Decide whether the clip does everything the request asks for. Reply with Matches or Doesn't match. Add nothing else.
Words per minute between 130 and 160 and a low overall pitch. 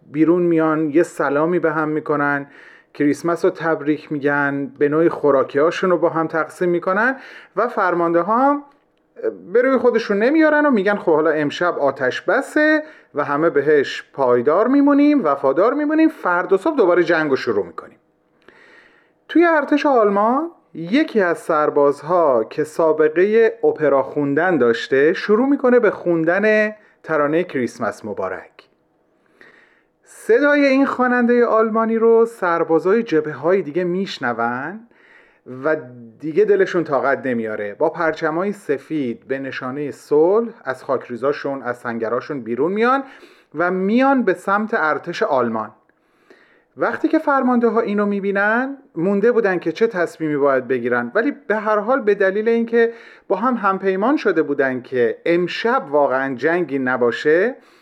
Doesn't match